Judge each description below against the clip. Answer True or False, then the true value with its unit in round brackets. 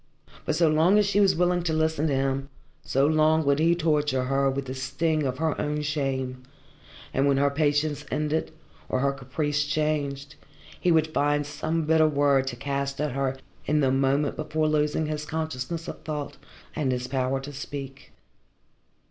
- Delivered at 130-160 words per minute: False (180 wpm)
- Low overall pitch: False (145 Hz)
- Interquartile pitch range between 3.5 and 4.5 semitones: False (2.4 semitones)